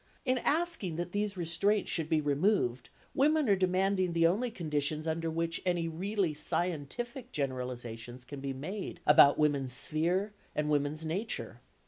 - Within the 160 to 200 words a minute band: No, average, 145 wpm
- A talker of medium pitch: Yes, medium, 165 Hz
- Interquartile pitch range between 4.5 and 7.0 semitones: Yes, average, 5.3 semitones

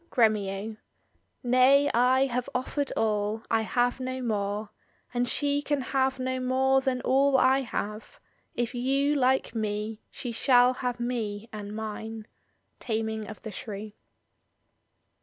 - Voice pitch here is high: Yes, high, 245 Hz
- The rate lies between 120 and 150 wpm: Yes, average, 140 wpm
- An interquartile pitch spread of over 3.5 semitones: No, average, 3.2 semitones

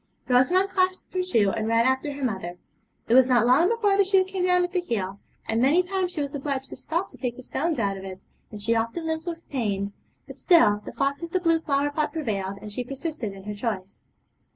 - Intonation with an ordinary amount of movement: No, wide, 7.7 semitones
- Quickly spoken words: Yes, fast, 240 wpm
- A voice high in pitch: Yes, very high, 275 Hz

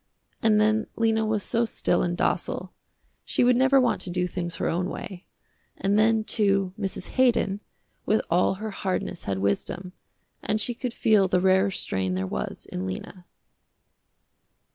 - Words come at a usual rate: Yes, average, 165 wpm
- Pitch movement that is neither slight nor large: Yes, average, 3.6 semitones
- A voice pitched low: No, high, 195 Hz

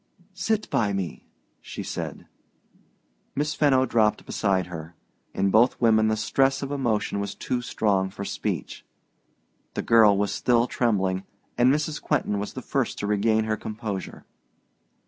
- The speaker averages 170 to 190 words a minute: No, average, 145 wpm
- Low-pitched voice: Yes, low, 110 Hz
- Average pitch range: Yes, average, 4.0 semitones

